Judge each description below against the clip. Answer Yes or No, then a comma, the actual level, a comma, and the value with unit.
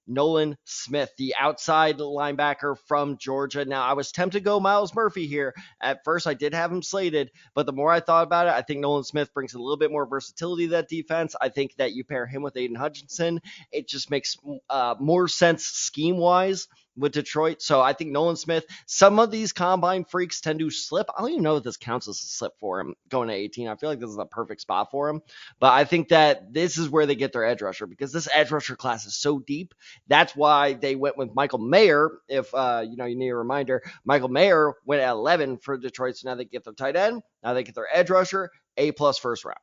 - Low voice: No, medium, 145 Hz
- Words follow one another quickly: Yes, fast, 240 wpm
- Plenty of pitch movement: No, average, 3.8 semitones